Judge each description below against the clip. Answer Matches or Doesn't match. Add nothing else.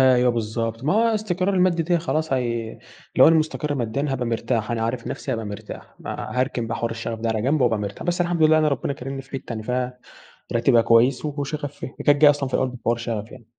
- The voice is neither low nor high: Doesn't match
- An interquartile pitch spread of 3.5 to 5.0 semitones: Matches